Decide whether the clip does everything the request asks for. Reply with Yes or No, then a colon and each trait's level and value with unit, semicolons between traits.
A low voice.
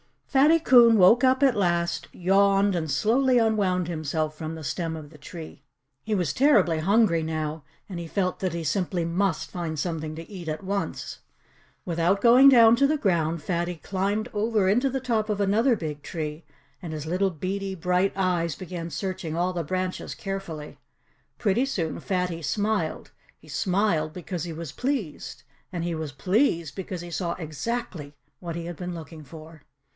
No: medium, 180 Hz